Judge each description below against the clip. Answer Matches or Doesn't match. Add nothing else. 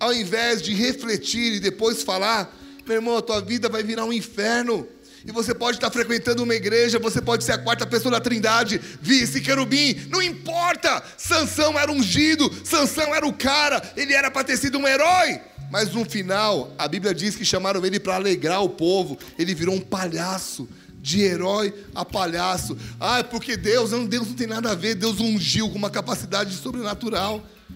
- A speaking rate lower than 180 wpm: Doesn't match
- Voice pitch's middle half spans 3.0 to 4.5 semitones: Matches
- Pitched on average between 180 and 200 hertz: Doesn't match